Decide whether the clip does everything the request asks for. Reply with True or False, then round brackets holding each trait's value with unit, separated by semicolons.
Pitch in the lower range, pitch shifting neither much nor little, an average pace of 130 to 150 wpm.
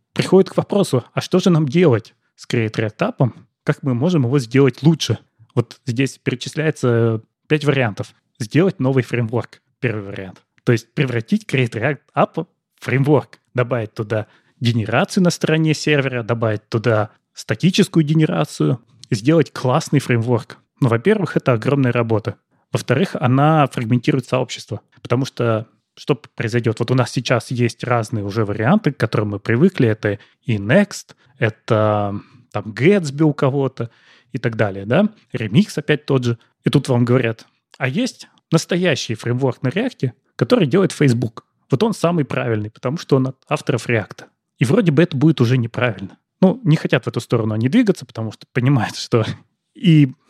False (130 Hz; 4.7 semitones; 160 wpm)